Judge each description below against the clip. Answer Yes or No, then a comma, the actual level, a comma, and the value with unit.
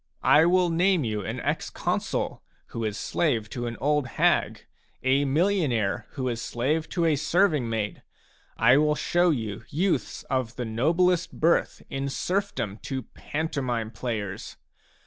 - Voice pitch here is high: No, low, 135 Hz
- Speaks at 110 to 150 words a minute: Yes, average, 145 wpm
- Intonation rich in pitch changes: Yes, wide, 6.1 semitones